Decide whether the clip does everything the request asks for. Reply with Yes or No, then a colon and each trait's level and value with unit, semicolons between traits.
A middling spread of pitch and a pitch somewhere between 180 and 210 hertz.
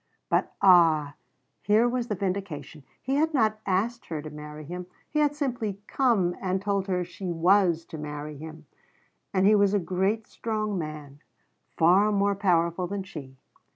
Yes: average, 4.5 semitones; high, 190 Hz